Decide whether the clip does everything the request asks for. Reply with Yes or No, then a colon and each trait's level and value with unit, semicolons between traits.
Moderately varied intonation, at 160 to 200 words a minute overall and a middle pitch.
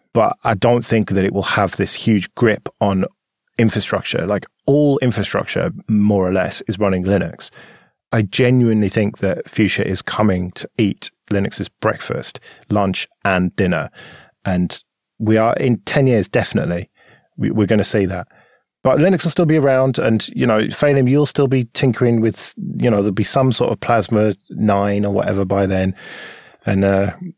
No: average, 4.0 semitones; average, 175 wpm; low, 110 Hz